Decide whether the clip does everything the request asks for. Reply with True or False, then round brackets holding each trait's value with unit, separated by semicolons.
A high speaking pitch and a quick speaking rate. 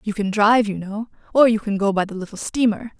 True (210 Hz; 260 wpm)